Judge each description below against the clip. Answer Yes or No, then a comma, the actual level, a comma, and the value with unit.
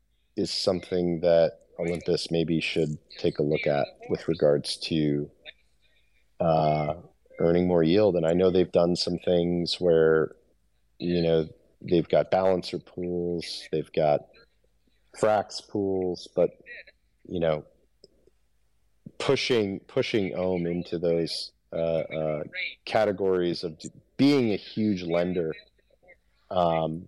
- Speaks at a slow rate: Yes, slow, 115 wpm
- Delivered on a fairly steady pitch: Yes, narrow, 2.1 semitones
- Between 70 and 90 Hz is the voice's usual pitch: Yes, very low, 85 Hz